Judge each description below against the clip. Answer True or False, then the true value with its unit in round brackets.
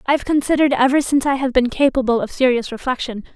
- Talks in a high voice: True (260 Hz)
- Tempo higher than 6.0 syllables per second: True (7.1 syllables/s)